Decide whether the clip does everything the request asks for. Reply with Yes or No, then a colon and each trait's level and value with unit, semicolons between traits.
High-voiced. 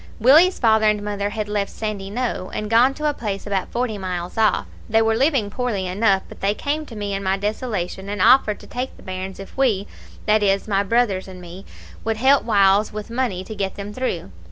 Yes: high, 210 Hz